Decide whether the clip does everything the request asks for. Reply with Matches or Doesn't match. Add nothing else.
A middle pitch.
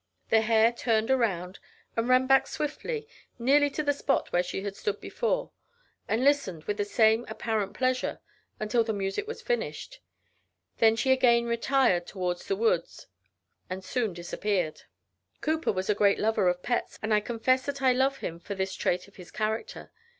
Doesn't match